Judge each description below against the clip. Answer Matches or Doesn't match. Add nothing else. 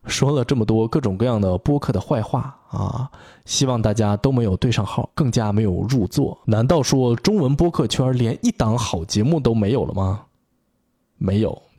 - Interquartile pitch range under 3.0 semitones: Doesn't match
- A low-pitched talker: Matches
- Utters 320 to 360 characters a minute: Doesn't match